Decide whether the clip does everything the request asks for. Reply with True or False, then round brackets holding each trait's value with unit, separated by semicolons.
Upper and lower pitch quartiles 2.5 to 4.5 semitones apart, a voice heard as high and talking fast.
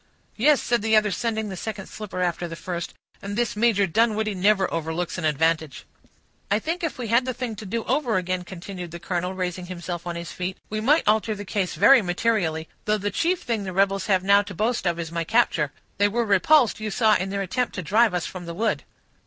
True (3.8 semitones; 200 Hz; 225 wpm)